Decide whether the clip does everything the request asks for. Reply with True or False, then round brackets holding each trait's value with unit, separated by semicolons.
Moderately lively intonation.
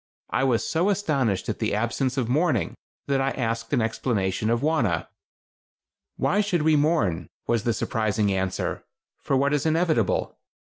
False (5.7 semitones)